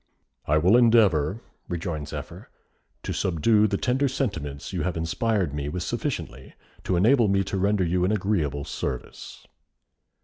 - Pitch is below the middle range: Yes, very low, 95 Hz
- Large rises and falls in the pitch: Yes, wide, 5.7 semitones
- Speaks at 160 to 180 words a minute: No, average, 145 wpm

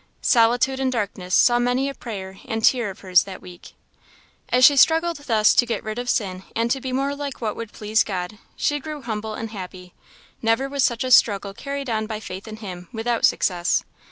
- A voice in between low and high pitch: No, high, 225 Hz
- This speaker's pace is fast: Yes, fast, 210 wpm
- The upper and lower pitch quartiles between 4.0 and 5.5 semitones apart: Yes, average, 4.3 semitones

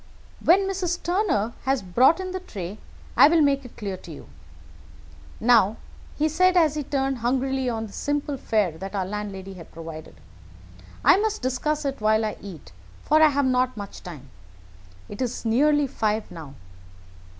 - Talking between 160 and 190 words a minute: Yes, average, 170 wpm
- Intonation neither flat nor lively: No, wide, 6.7 semitones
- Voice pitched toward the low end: No, very high, 250 Hz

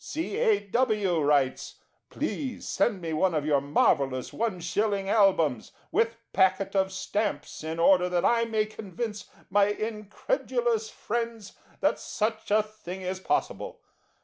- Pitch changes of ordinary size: Yes, average, 4.1 semitones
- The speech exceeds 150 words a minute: No, slow, 135 wpm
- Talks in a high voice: Yes, high, 200 Hz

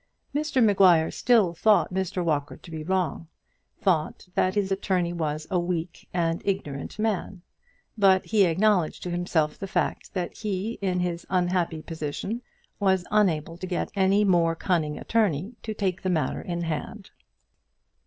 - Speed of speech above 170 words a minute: No, average, 155 wpm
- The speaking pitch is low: No, medium, 180 Hz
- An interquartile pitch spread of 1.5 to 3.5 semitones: Yes, average, 3.0 semitones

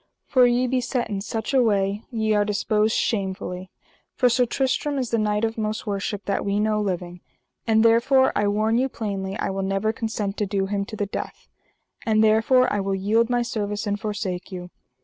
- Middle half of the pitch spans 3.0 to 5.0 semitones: No, narrow, 2.6 semitones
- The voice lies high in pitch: Yes, high, 215 Hz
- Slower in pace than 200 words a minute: No, fast, 205 wpm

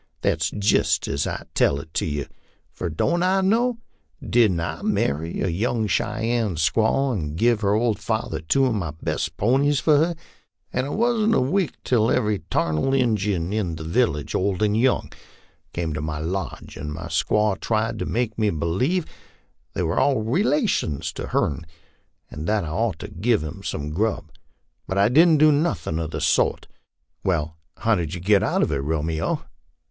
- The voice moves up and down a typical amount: No, wide, 7.3 semitones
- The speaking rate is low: No, average, 185 wpm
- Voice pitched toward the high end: No, low, 105 Hz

